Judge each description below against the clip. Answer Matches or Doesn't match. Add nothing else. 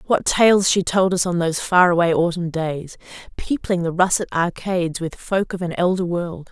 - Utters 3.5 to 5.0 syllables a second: Matches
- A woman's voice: Matches